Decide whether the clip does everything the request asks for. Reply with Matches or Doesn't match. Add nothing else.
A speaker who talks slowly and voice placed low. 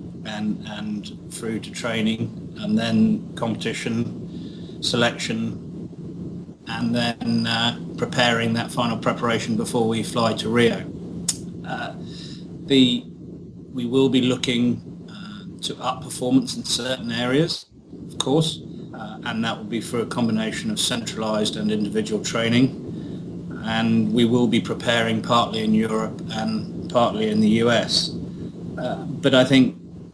Matches